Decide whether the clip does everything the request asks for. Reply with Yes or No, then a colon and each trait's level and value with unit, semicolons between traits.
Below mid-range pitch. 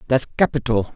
Yes: low, 125 Hz